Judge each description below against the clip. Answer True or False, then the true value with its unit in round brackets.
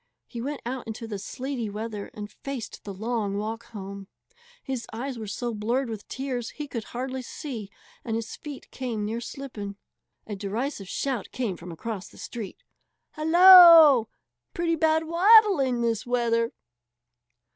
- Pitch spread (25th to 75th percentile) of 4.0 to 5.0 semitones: True (4.4 semitones)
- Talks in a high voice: True (235 Hz)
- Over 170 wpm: False (150 wpm)